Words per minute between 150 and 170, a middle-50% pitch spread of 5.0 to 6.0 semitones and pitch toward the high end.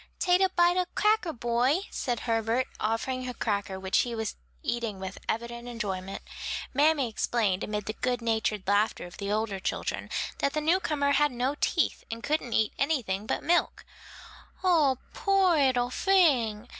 Yes: average, 160 wpm; wide, 5.5 semitones; high, 240 Hz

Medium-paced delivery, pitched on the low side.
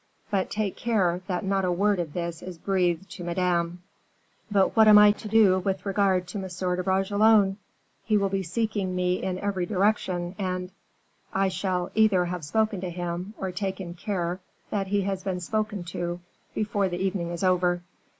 No: average, 185 wpm; high, 190 Hz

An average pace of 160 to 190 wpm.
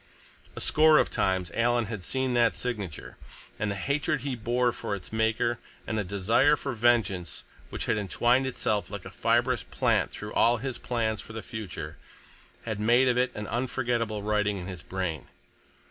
Yes: average, 175 wpm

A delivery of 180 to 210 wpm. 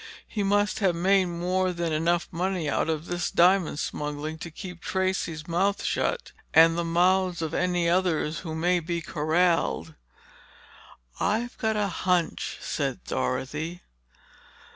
No: slow, 135 wpm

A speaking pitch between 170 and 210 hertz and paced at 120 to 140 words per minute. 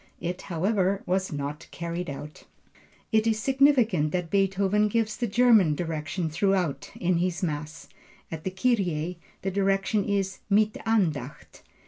Yes: medium, 185 Hz; slow, 135 wpm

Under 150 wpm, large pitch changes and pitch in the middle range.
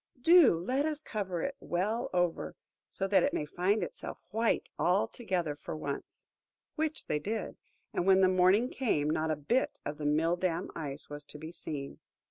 No: average, 180 wpm; wide, 5.8 semitones; medium, 180 Hz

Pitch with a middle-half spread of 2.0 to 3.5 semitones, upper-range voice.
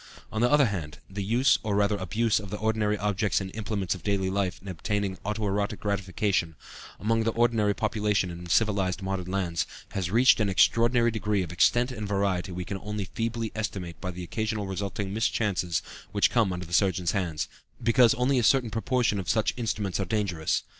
No: average, 2.8 semitones; low, 100 Hz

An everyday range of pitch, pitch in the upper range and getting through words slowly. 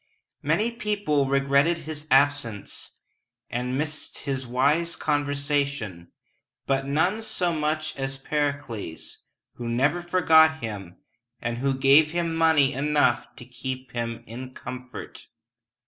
No: average, 3.6 semitones; medium, 140 Hz; slow, 115 wpm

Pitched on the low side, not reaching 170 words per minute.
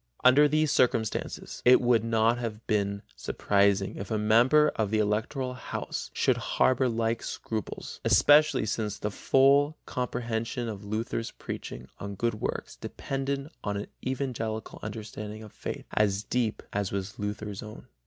Yes: low, 110 Hz; average, 145 wpm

